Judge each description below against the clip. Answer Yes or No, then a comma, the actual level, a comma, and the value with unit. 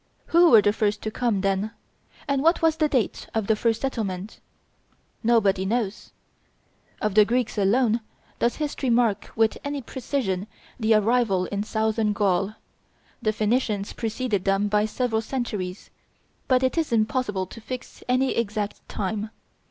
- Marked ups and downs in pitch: No, average, 3.3 semitones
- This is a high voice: Yes, high, 220 Hz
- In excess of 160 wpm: No, average, 150 wpm